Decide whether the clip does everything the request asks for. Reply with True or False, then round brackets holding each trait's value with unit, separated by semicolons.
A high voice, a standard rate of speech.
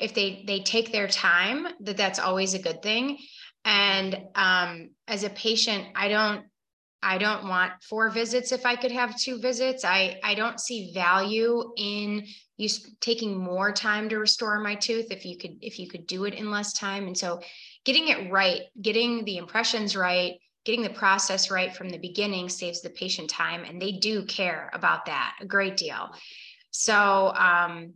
True (205 Hz; 185 wpm)